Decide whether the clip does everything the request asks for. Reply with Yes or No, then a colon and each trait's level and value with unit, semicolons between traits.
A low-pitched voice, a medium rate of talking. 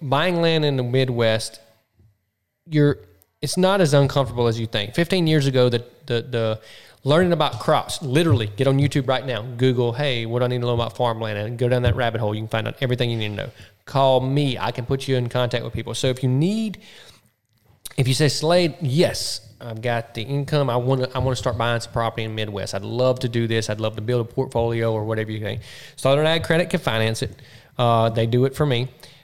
No: low, 125 Hz; fast, 240 wpm